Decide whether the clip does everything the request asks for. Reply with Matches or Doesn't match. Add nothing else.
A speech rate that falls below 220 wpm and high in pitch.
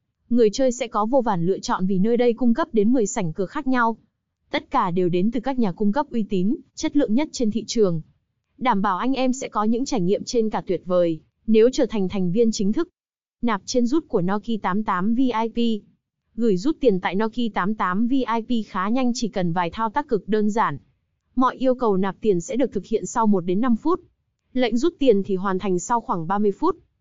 Doesn't match